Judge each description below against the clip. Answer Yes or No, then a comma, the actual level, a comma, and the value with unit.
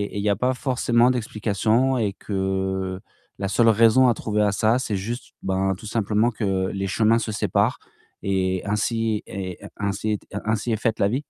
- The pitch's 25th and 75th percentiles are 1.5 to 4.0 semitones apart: Yes, average, 2.8 semitones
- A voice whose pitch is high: No, low, 105 Hz